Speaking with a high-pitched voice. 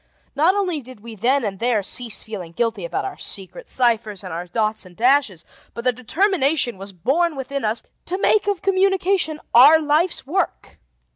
Yes: very high, 255 Hz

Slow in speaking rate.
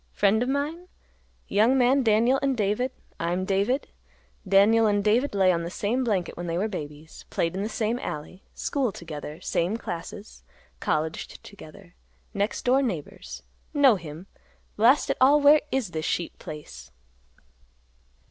No: average, 155 wpm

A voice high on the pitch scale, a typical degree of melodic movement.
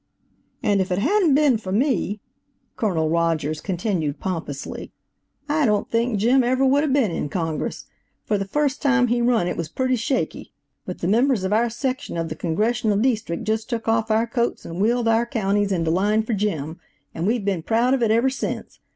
Yes: high, 220 Hz; average, 5.0 semitones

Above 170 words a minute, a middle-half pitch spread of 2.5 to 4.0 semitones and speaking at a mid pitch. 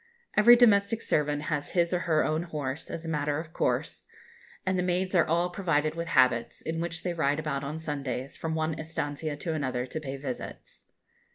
Yes: average, 195 wpm; average, 2.9 semitones; medium, 160 Hz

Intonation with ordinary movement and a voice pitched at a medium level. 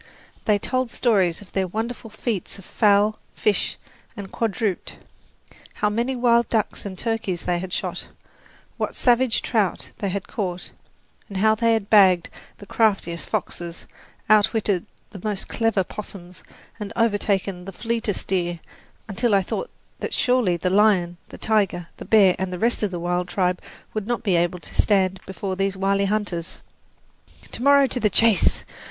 No: average, 3.3 semitones; high, 200 Hz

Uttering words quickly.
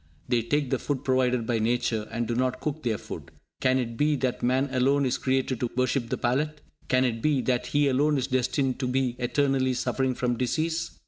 Yes: fast, 210 wpm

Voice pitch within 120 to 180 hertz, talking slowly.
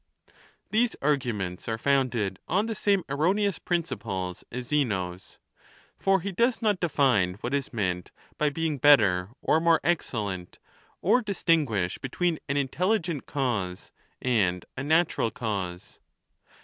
Yes: medium, 140 Hz; slow, 125 wpm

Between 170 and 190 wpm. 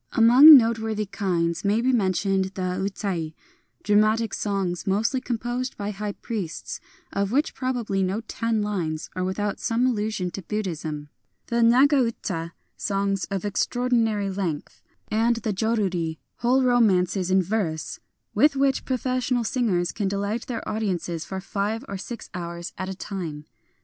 No: average, 150 wpm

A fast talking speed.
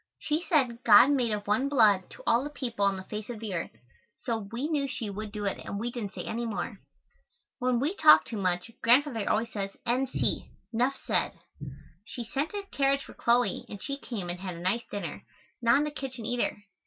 Yes: fast, 215 wpm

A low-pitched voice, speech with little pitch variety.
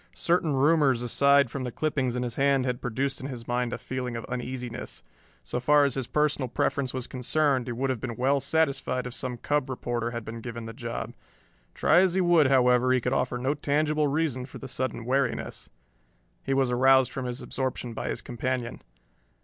Yes: low, 130 Hz; narrow, 2.3 semitones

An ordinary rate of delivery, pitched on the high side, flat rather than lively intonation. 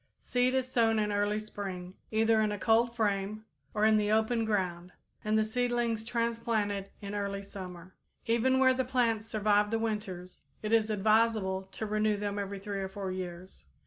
Yes: average, 175 wpm; high, 215 Hz; narrow, 2.3 semitones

